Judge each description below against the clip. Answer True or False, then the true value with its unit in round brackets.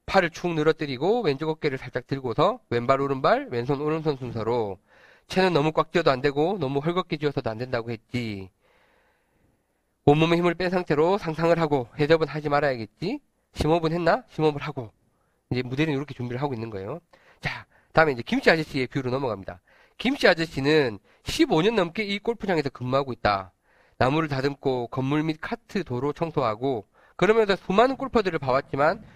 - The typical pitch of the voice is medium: True (145 Hz)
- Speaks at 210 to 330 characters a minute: False (375 characters per minute)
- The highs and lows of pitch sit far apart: False (4.8 semitones)